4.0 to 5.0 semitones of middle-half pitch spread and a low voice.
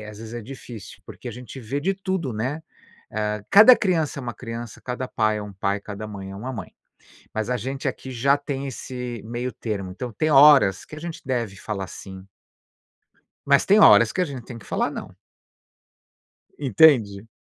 Yes: average, 4.7 semitones; low, 120 Hz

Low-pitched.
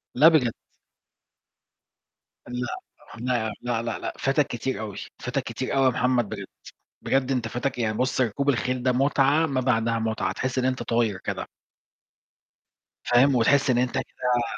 Yes: low, 125 Hz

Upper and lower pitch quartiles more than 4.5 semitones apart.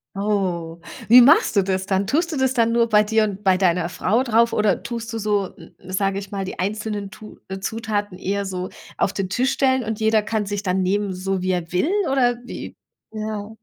No: average, 2.9 semitones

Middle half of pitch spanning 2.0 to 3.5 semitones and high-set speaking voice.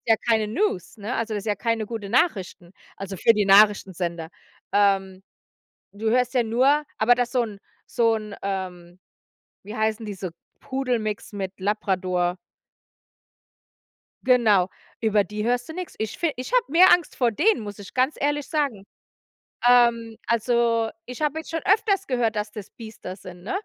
No: average, 3.9 semitones; high, 220 Hz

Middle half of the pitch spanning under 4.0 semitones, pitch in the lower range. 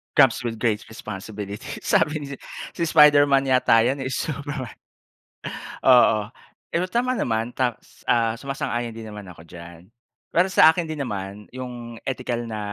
No: average, 4.4 semitones; low, 120 Hz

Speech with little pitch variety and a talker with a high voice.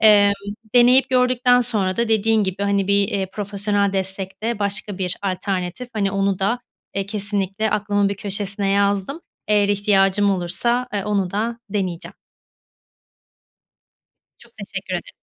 Yes: narrow, 1.8 semitones; high, 200 Hz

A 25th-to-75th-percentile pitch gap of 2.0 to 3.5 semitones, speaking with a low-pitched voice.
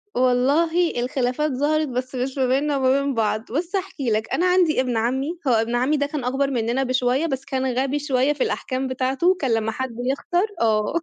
No: average, 2.9 semitones; very high, 265 Hz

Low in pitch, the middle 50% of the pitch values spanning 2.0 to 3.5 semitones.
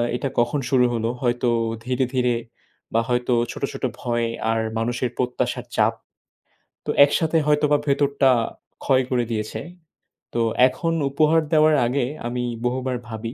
Yes: low, 125 Hz; average, 2.9 semitones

